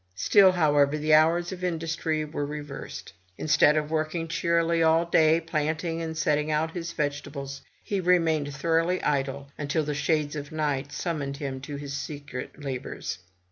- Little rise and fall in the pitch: Yes, narrow, 2.3 semitones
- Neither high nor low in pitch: Yes, medium, 155 Hz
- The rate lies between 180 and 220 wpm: No, average, 155 wpm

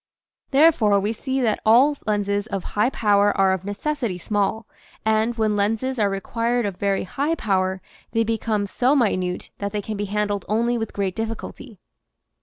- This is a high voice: Yes, high, 210 Hz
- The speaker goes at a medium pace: Yes, average, 170 wpm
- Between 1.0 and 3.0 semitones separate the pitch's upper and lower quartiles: Yes, narrow, 2.6 semitones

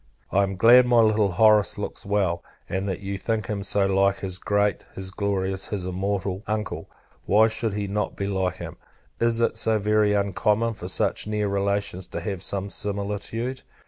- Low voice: Yes, low, 100 Hz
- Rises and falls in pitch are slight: Yes, narrow, 1.8 semitones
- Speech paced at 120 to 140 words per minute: No, average, 185 wpm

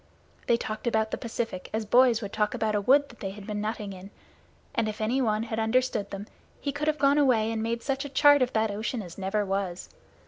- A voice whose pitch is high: Yes, high, 220 Hz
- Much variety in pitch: No, average, 3.4 semitones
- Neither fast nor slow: No, fast, 235 wpm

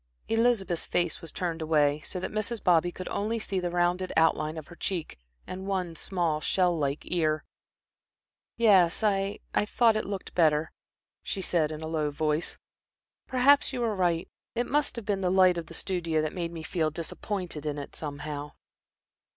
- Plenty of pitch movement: No, average, 3.8 semitones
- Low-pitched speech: No, medium, 175 Hz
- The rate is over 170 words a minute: Yes, average, 185 wpm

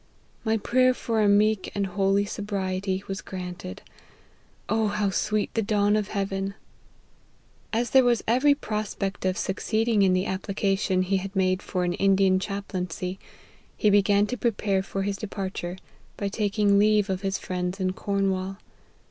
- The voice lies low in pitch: No, high, 200 Hz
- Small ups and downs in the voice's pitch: Yes, narrow, 1.9 semitones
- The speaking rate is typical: Yes, average, 155 wpm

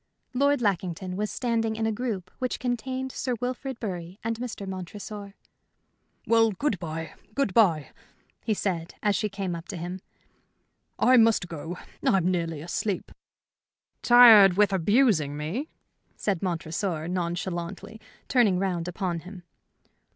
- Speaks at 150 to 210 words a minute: No, slow, 135 wpm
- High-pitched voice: Yes, high, 195 Hz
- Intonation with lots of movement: No, average, 4.5 semitones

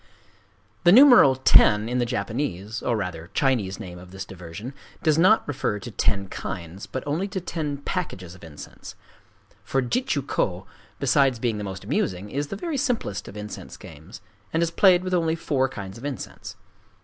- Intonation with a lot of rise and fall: Yes, wide, 8.8 semitones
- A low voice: Yes, low, 120 Hz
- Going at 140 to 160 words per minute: No, average, 175 wpm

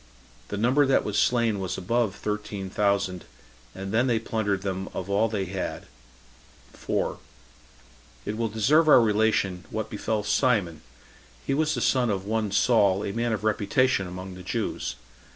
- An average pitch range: Yes, average, 3.1 semitones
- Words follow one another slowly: No, average, 165 wpm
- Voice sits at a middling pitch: No, low, 105 Hz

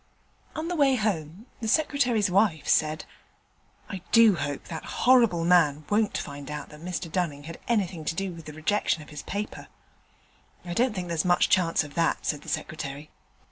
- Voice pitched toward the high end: No, medium, 175 Hz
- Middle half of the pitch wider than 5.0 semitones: Yes, wide, 5.5 semitones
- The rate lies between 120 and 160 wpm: No, average, 180 wpm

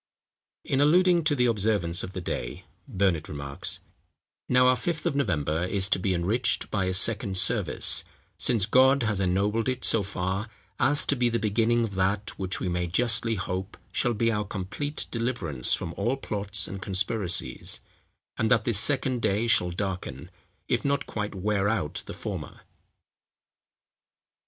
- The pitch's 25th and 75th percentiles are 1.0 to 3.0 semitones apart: No, average, 4.3 semitones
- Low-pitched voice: Yes, low, 105 Hz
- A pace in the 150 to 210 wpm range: Yes, average, 160 wpm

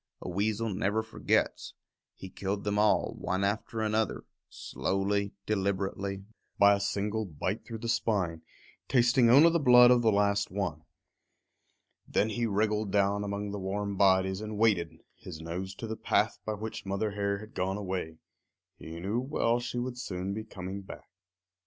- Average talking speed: Yes, average, 165 wpm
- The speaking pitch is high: No, low, 100 Hz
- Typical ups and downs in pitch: No, narrow, 2.3 semitones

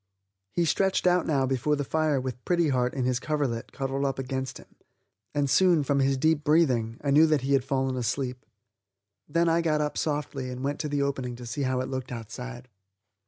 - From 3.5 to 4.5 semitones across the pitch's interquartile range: No, average, 2.8 semitones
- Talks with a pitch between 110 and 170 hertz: Yes, low, 135 Hz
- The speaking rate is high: Yes, fast, 210 wpm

